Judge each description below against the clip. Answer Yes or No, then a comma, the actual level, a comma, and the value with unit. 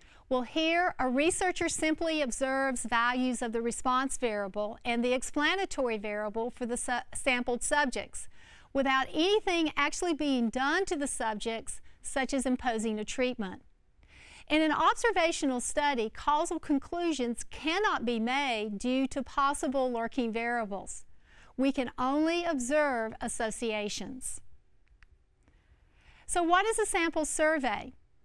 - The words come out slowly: Yes, slow, 125 wpm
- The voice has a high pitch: Yes, very high, 265 Hz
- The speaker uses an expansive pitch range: No, average, 4.6 semitones